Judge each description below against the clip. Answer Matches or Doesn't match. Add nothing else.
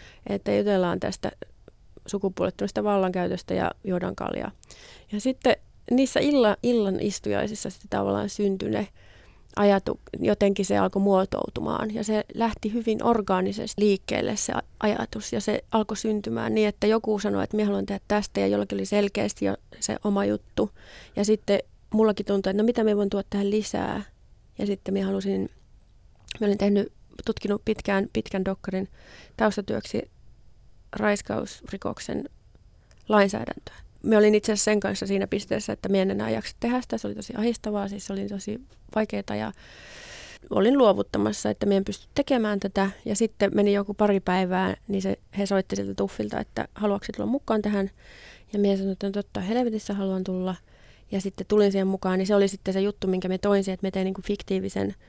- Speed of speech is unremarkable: Doesn't match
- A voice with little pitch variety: Matches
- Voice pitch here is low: Doesn't match